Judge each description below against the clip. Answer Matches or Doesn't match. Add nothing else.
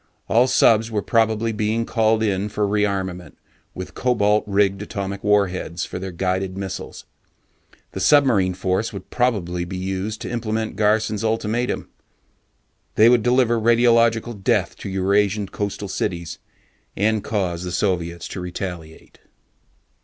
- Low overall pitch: Matches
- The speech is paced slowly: Matches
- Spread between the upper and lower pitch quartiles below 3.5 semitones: Matches